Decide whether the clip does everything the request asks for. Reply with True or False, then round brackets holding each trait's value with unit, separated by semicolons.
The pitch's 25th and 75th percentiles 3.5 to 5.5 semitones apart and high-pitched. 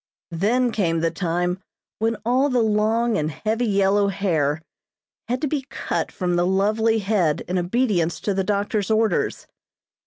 True (4.2 semitones; 205 Hz)